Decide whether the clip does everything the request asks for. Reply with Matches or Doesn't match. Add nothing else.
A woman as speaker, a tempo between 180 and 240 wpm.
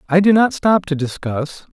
Doesn't match